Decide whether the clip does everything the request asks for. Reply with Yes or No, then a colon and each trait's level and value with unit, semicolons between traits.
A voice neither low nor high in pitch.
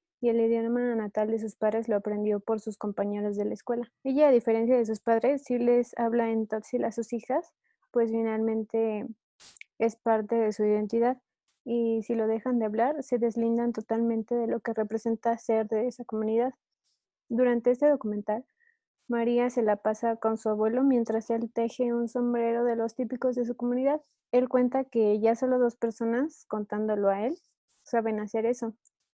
No: high, 230 Hz